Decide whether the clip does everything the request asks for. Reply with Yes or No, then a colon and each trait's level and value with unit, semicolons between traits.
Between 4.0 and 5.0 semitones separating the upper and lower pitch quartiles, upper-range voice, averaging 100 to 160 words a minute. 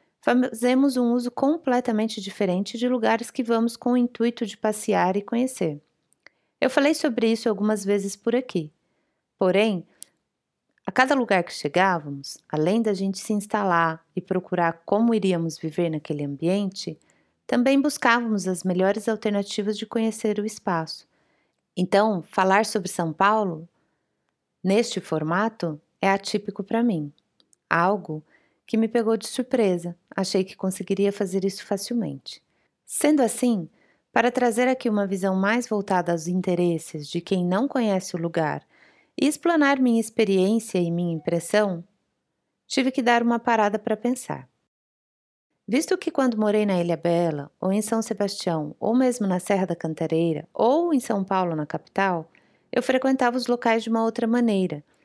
Yes: average, 4.7 semitones; high, 205 Hz; average, 150 wpm